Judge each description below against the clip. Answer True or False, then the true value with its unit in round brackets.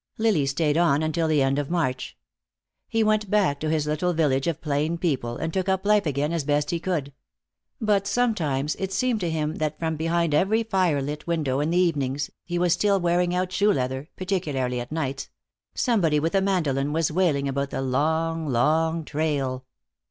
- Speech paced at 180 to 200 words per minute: True (190 wpm)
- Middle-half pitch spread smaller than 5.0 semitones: True (4.0 semitones)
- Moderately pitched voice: True (160 Hz)